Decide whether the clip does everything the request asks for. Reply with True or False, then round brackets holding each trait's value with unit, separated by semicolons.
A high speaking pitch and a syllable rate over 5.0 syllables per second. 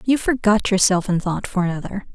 True (200 Hz; 5.5 syllables/s)